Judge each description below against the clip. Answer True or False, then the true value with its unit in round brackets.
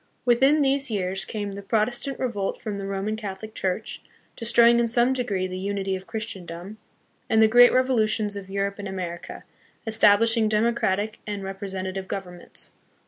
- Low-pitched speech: False (210 Hz)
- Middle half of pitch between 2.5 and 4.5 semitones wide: True (3.1 semitones)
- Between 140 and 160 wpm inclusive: True (155 wpm)